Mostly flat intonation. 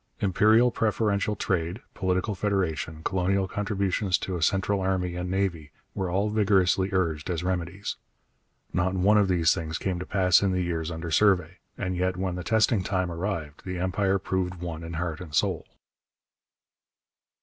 Yes: narrow, 2.1 semitones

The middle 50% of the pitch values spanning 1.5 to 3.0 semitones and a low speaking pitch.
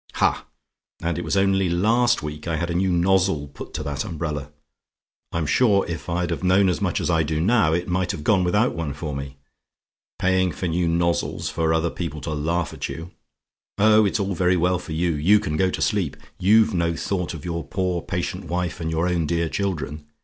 Yes: average, 2.7 semitones; very low, 85 Hz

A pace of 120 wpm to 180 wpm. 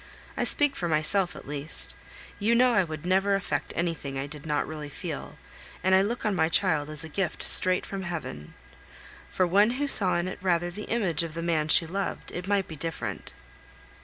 No: fast, 205 wpm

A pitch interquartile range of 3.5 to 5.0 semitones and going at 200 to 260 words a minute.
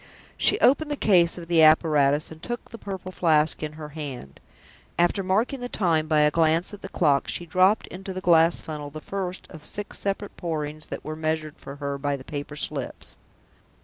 Yes: average, 3.8 semitones; fast, 205 wpm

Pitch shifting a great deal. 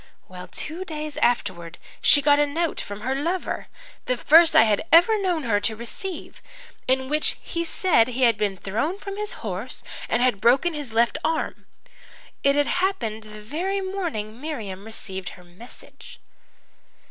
Yes: wide, 7.4 semitones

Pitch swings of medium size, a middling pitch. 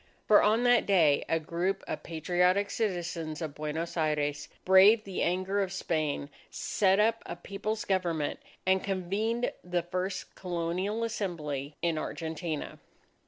Yes: average, 3.6 semitones; medium, 180 Hz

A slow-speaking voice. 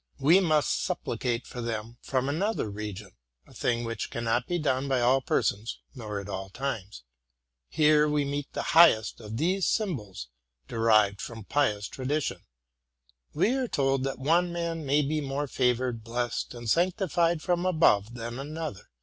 No: average, 160 wpm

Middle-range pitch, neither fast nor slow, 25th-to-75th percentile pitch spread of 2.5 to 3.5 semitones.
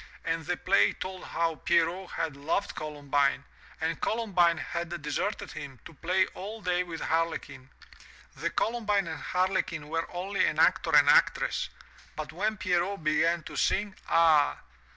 Yes: medium, 170 Hz; average, 150 wpm; average, 2.9 semitones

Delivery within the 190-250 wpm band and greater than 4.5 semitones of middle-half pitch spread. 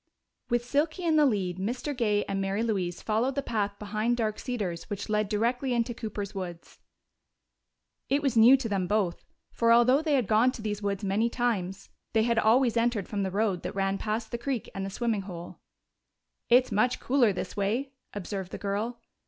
No: average, 195 wpm; average, 3.4 semitones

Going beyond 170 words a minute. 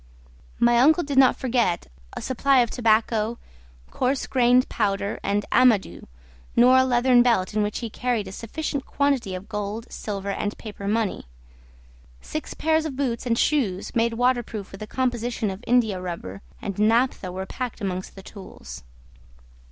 No: average, 155 wpm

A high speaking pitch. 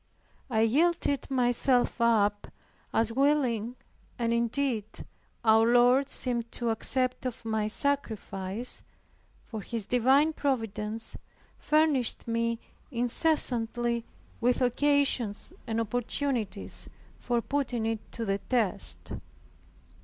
Yes: high, 235 Hz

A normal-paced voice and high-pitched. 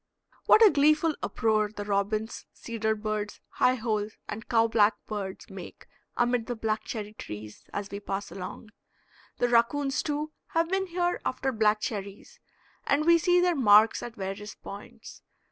Yes: average, 160 wpm; high, 220 Hz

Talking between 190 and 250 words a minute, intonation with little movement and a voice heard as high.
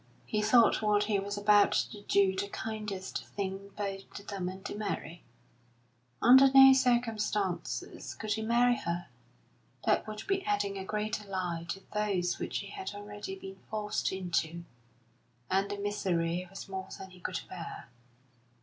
No: average, 160 wpm; narrow, 2.0 semitones; high, 205 Hz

